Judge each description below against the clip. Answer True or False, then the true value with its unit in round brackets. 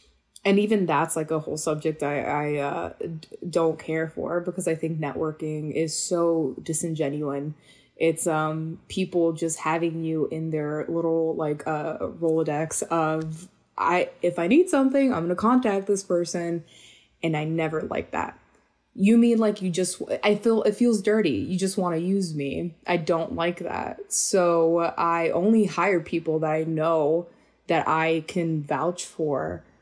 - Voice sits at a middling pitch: True (165 Hz)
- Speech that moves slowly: False (165 wpm)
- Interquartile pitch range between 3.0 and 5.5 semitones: False (2.4 semitones)